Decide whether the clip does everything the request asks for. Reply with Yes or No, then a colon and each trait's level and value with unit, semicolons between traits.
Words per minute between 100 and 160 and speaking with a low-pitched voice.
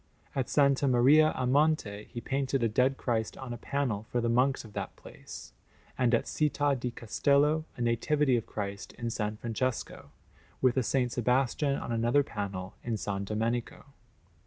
No: average, 170 wpm; low, 120 Hz